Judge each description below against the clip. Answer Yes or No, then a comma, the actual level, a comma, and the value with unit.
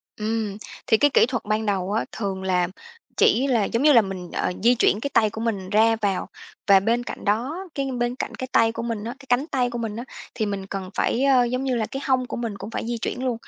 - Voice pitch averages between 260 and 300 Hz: No, high, 225 Hz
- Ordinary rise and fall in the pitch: Yes, average, 3.3 semitones